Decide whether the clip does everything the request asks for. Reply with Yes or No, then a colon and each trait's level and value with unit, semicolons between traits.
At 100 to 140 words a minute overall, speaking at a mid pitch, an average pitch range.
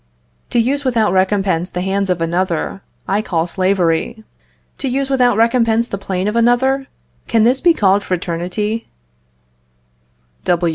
No: slow, 135 wpm; high, 205 Hz; average, 4.4 semitones